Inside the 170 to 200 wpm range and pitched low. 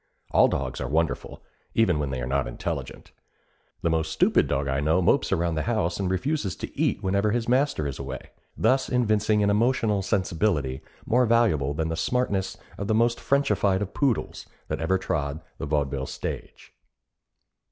Yes: average, 175 wpm; very low, 95 Hz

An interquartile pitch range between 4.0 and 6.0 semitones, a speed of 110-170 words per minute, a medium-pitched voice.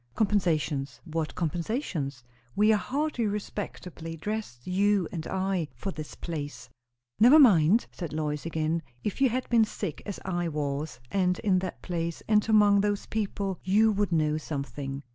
Yes: average, 5.0 semitones; average, 155 wpm; medium, 180 Hz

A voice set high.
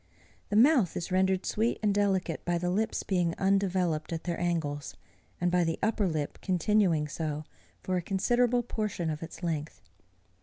No: medium, 180 Hz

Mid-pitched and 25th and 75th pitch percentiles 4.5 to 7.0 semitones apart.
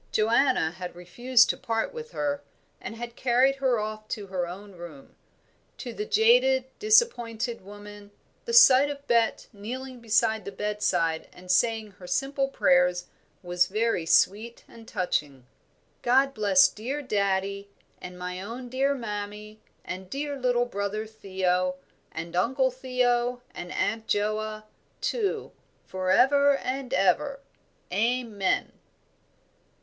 No: high, 220 Hz; average, 5.1 semitones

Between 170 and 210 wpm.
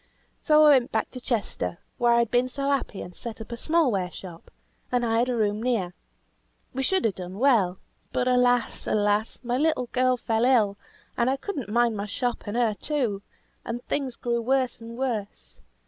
Yes: average, 195 wpm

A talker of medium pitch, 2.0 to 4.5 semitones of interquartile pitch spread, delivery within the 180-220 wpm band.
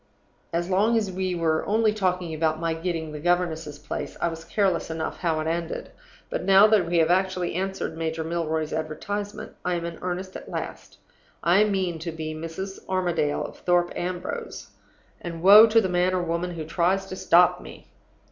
Yes: medium, 175 Hz; narrow, 2.5 semitones; average, 185 wpm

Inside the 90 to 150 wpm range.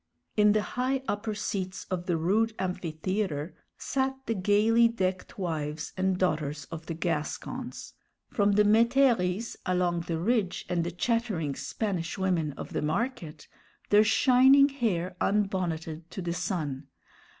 Yes: average, 140 wpm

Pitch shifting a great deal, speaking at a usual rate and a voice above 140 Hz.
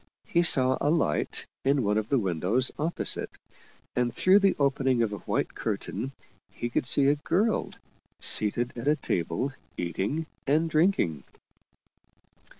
No: wide, 6.1 semitones; average, 145 wpm; low, 130 Hz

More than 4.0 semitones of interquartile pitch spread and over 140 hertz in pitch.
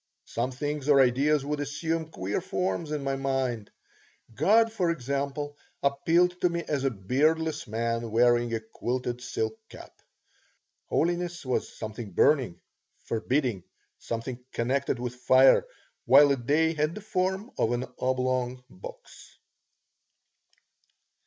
No: average, 4.5 semitones; low, 135 Hz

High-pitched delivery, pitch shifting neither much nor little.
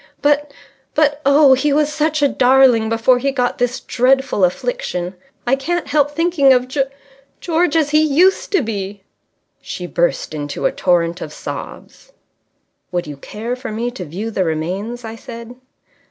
No: very high, 255 Hz; wide, 6.0 semitones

